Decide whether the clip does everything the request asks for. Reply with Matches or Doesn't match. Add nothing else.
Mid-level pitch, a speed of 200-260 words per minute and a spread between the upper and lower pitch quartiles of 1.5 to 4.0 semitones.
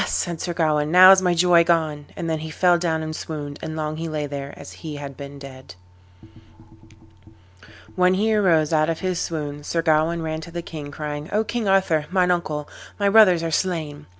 Matches